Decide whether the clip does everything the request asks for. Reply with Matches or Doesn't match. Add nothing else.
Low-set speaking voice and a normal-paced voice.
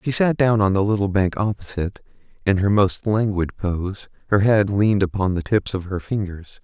Matches